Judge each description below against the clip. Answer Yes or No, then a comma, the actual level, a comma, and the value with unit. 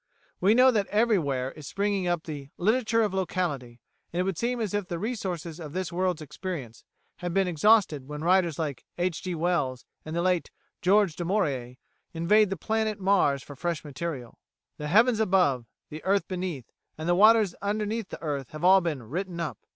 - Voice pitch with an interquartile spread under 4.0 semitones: No, average, 4.7 semitones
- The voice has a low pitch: No, medium, 180 Hz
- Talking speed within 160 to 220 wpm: Yes, average, 190 wpm